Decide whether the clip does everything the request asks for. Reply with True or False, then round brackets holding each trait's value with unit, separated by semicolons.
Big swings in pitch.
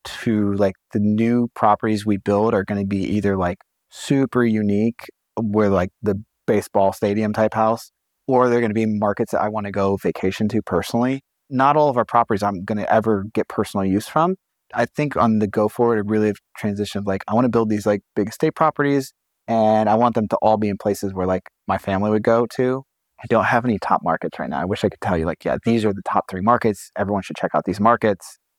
False (2.4 semitones)